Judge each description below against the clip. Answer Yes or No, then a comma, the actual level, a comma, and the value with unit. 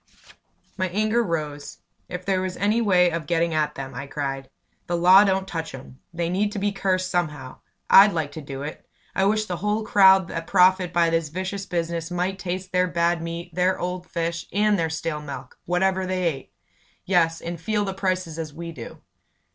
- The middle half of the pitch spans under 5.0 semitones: Yes, narrow, 2.5 semitones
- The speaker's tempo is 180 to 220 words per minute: Yes, average, 195 wpm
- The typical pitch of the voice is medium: Yes, medium, 175 Hz